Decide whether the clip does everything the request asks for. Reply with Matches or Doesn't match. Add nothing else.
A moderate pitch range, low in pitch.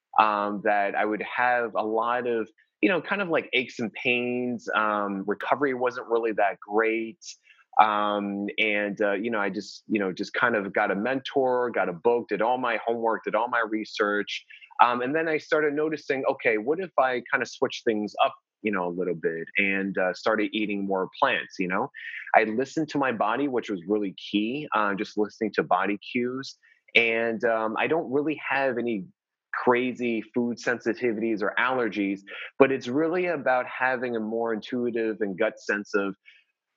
Matches